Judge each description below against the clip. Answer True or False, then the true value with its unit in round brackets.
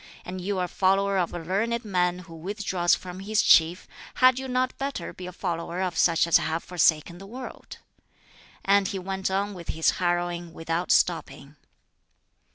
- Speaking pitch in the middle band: True (180 Hz)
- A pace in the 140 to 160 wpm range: False (175 wpm)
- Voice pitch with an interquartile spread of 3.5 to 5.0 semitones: False (2.5 semitones)